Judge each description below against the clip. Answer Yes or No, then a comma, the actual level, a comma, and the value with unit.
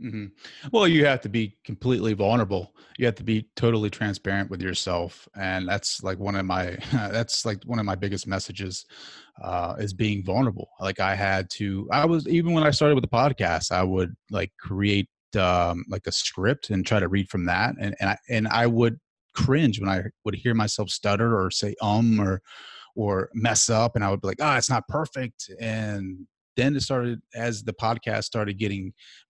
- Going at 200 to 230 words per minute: Yes, fast, 205 wpm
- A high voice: No, low, 105 Hz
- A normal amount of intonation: Yes, average, 3.4 semitones